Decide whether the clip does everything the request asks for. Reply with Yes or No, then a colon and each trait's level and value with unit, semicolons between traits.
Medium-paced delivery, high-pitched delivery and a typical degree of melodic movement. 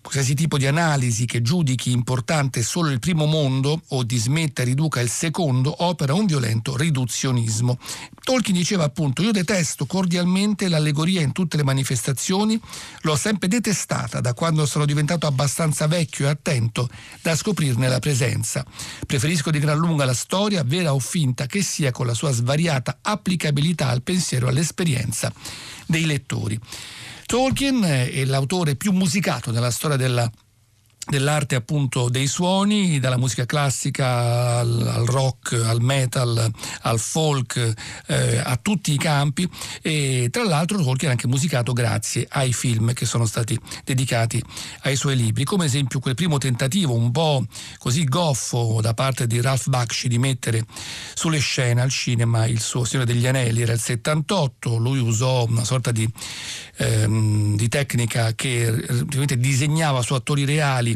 No: average, 155 wpm; low, 135 Hz; average, 4.4 semitones